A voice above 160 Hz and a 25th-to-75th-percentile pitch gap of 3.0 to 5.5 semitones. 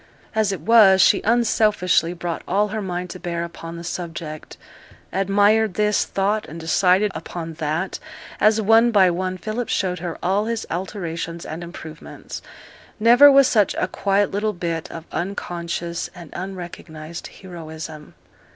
Yes: medium, 185 Hz; average, 3.7 semitones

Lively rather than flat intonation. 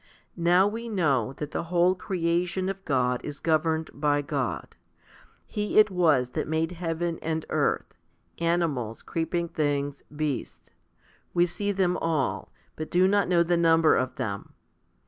No: average, 3.6 semitones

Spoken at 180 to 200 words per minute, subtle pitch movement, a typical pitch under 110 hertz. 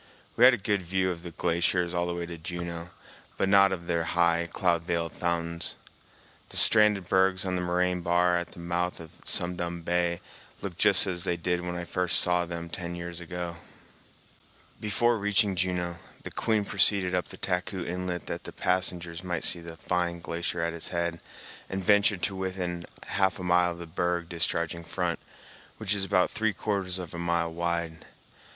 Yes: average, 190 wpm; narrow, 1.5 semitones; very low, 90 Hz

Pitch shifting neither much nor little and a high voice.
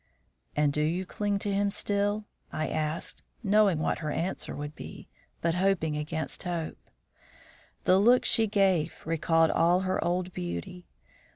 No: average, 4.1 semitones; medium, 175 Hz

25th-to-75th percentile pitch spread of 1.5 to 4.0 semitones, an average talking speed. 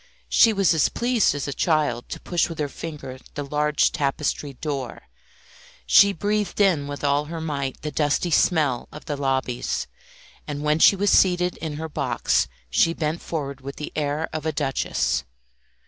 Yes: average, 2.9 semitones; average, 175 wpm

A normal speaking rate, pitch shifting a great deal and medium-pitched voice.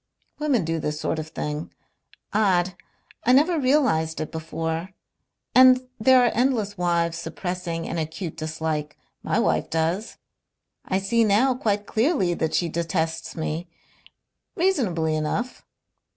No: slow, 130 wpm; wide, 6.4 semitones; medium, 175 Hz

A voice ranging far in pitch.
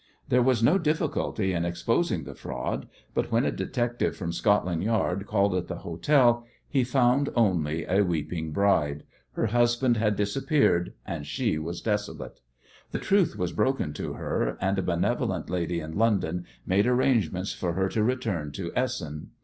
Yes: wide, 6.0 semitones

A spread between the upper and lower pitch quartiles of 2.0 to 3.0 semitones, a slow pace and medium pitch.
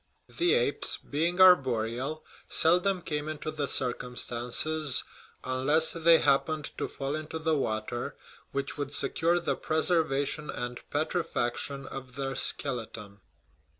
No: average, 3.7 semitones; slow, 120 wpm; medium, 145 Hz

